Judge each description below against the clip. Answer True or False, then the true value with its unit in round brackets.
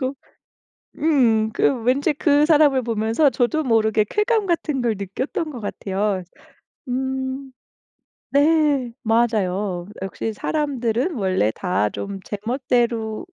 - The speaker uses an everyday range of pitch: True (4.9 semitones)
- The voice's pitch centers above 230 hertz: True (240 Hz)